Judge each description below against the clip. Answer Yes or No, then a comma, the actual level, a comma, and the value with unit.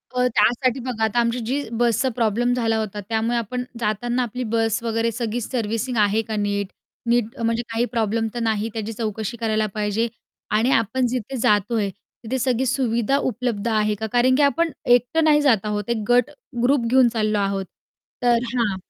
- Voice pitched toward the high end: Yes, high, 230 Hz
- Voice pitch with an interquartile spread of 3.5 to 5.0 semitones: No, narrow, 2.4 semitones